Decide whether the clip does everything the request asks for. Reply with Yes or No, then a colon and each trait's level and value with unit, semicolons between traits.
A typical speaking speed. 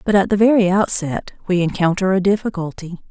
Yes: average, 175 wpm